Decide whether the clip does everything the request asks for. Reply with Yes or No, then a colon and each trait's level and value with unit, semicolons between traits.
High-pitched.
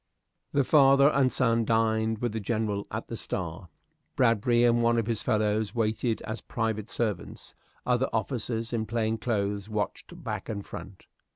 No: low, 110 Hz